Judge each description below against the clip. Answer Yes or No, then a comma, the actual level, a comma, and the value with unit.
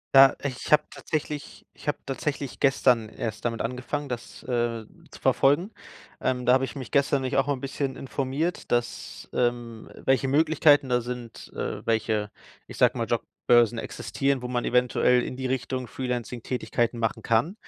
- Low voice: Yes, low, 125 Hz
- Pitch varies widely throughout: No, narrow, 2.4 semitones